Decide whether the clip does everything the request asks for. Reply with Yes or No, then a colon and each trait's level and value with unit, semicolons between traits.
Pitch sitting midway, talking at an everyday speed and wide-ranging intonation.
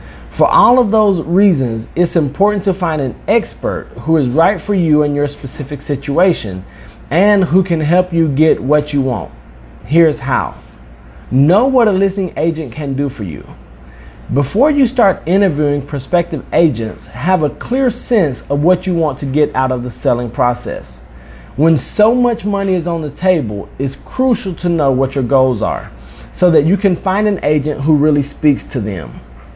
Yes: medium, 150 Hz; average, 180 wpm; wide, 6.5 semitones